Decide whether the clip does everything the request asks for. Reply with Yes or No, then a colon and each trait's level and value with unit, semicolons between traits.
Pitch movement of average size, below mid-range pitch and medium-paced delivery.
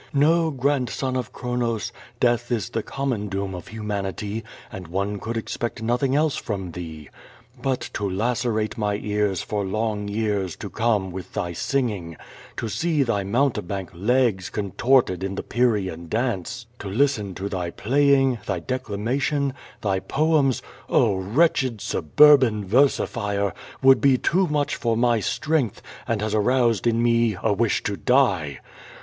Yes: average, 4.5 semitones; low, 110 Hz; average, 150 wpm